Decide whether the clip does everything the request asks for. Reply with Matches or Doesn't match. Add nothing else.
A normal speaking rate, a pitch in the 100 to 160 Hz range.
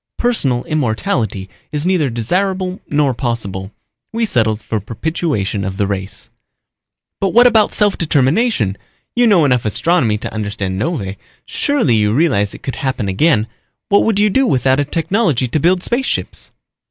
Matches